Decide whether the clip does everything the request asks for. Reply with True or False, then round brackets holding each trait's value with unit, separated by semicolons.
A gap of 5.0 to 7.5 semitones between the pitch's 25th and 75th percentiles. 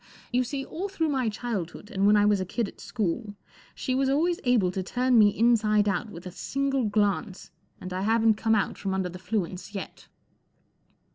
False (4.3 semitones)